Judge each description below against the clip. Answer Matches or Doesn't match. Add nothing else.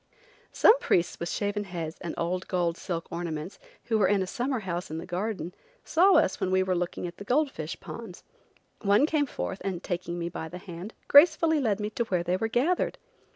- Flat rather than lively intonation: Doesn't match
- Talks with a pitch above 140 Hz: Matches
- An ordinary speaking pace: Doesn't match